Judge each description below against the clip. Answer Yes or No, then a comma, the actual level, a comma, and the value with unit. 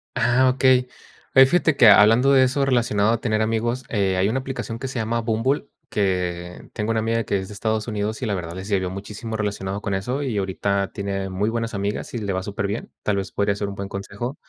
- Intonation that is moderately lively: Yes, average, 3.2 semitones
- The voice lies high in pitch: No, low, 110 Hz